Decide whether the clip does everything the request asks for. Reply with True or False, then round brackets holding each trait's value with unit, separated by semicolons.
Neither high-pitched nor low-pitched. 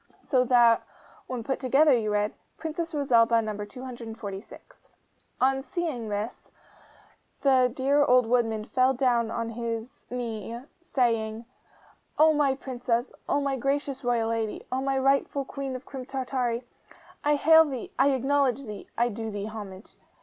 False (250 Hz)